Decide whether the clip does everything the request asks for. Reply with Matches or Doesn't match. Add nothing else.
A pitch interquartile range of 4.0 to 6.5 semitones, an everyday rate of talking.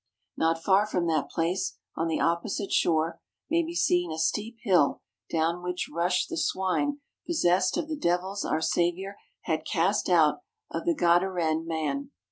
Doesn't match